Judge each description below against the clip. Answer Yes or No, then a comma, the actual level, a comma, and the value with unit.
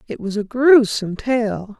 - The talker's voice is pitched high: Yes, high, 225 Hz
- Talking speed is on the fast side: No, average, 165 wpm